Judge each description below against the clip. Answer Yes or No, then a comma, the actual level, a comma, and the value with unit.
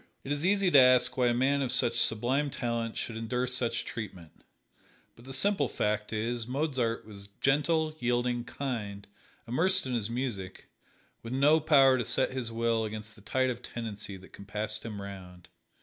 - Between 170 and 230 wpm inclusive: Yes, average, 175 wpm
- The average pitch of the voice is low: Yes, low, 120 Hz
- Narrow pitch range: No, average, 3.6 semitones